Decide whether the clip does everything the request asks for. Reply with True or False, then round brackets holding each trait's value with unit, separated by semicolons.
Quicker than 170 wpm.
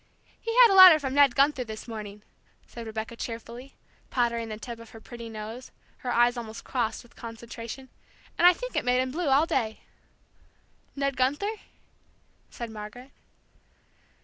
False (160 wpm)